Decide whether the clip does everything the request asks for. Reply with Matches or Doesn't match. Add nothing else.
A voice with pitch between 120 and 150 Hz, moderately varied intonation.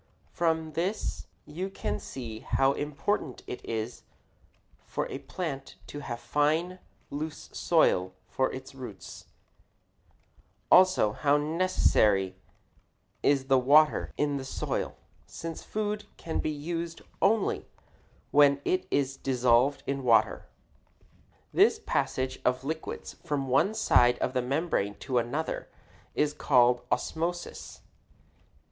Matches